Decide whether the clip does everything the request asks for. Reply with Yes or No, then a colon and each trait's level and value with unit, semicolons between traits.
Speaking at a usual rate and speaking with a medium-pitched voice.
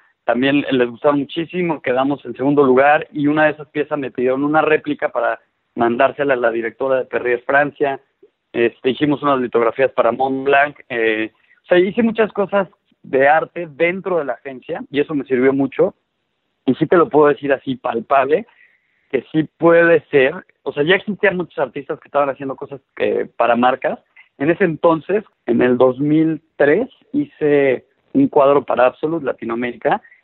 Yes: average, 170 wpm; medium, 145 Hz